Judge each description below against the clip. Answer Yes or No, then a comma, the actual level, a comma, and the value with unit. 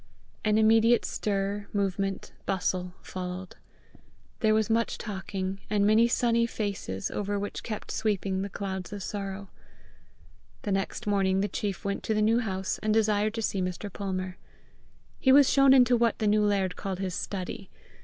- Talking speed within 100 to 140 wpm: No, average, 165 wpm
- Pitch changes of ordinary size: No, narrow, 2.3 semitones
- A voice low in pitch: No, high, 205 Hz